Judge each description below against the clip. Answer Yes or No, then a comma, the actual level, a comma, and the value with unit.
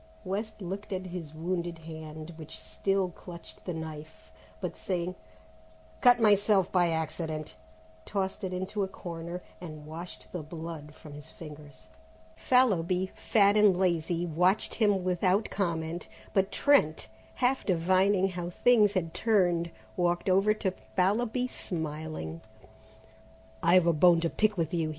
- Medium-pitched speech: Yes, medium, 180 Hz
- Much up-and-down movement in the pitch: No, average, 3.2 semitones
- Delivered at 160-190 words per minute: No, slow, 135 wpm